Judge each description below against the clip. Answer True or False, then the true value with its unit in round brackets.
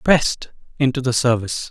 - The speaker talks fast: False (140 wpm)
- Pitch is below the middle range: True (130 Hz)